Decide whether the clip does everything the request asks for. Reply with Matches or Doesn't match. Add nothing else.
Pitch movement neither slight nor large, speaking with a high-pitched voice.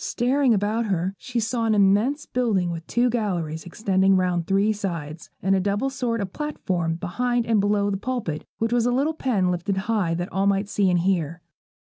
Matches